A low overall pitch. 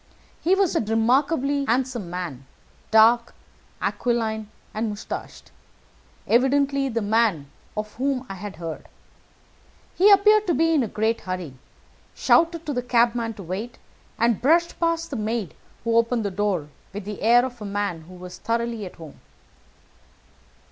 No: high, 230 Hz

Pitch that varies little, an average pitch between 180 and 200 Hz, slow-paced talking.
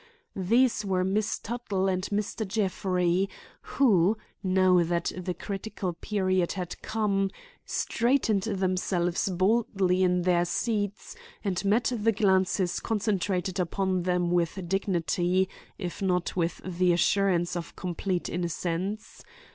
Yes: narrow, 2.3 semitones; high, 190 Hz; slow, 115 wpm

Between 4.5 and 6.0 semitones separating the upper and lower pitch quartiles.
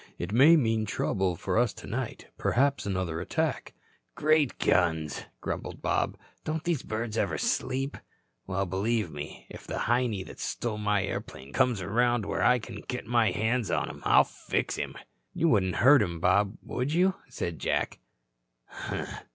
Yes: average, 5.0 semitones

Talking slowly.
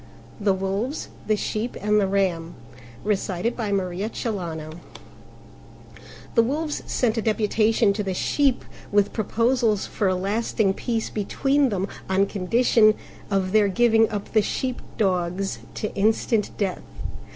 Yes: slow, 120 wpm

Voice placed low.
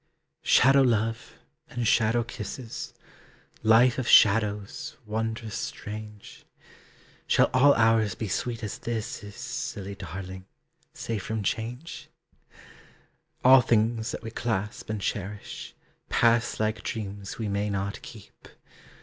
Yes: low, 110 Hz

